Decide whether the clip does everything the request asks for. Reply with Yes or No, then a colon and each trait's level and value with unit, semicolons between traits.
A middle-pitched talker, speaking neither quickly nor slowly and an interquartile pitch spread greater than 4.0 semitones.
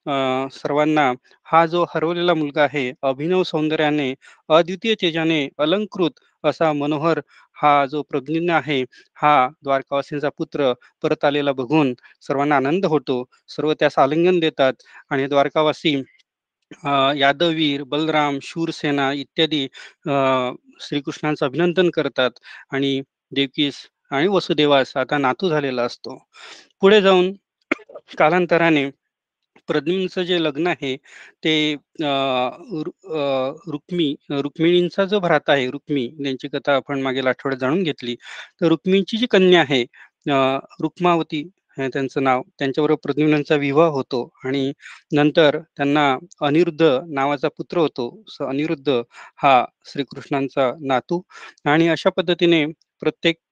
No: medium, 150 Hz; average, 110 wpm; average, 3.1 semitones